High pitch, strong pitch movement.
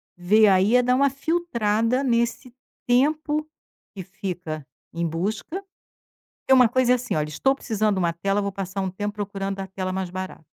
No: high, 205 Hz; average, 5.0 semitones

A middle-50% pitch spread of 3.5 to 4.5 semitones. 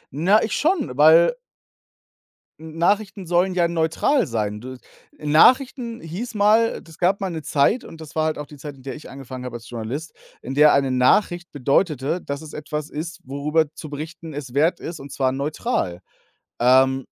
Yes: average, 4.2 semitones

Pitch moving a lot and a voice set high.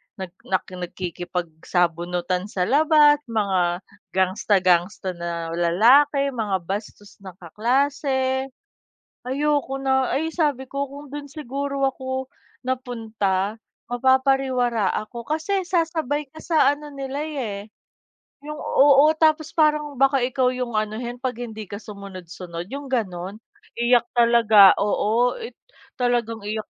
Yes: wide, 5.9 semitones; high, 245 Hz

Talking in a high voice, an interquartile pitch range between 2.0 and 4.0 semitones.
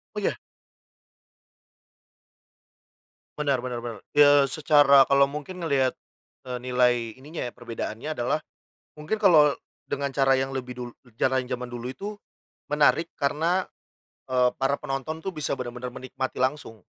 No: low, 135 Hz; average, 2.9 semitones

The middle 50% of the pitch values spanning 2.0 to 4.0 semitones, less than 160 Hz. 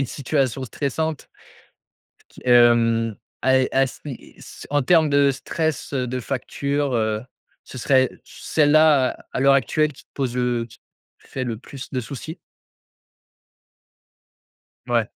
Yes: average, 2.8 semitones; low, 135 Hz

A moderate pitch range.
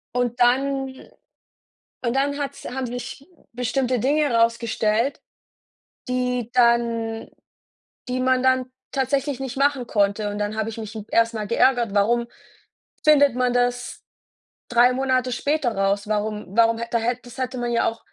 No: narrow, 2.2 semitones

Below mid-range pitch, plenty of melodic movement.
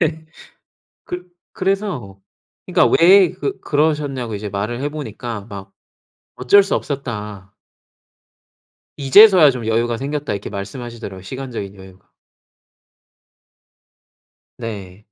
Yes: low, 120 Hz; wide, 6.8 semitones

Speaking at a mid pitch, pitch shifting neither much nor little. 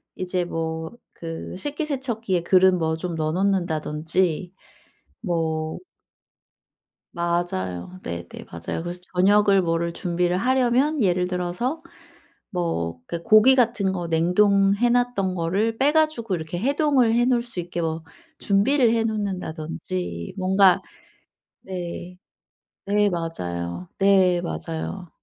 Yes: medium, 180 Hz; average, 4.5 semitones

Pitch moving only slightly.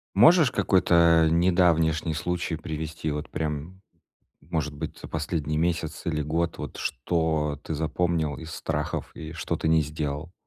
Yes: narrow, 1.9 semitones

